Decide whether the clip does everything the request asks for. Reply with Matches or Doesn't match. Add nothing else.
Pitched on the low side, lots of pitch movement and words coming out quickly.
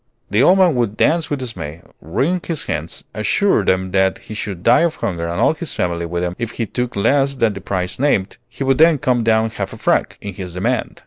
Matches